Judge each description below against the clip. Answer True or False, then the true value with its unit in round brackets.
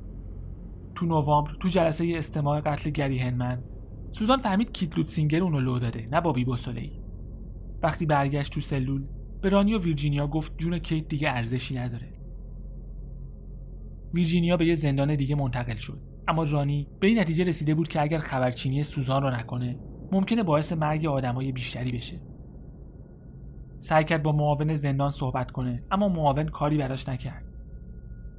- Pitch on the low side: False (145 Hz)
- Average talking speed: True (145 wpm)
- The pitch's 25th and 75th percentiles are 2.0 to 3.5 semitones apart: False (4.5 semitones)